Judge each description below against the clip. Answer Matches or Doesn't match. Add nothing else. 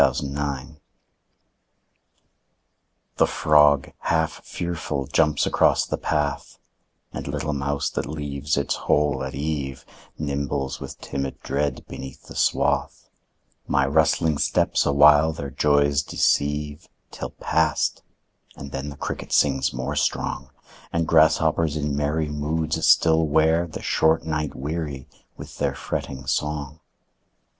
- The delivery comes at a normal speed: Doesn't match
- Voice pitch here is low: Matches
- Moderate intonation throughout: Doesn't match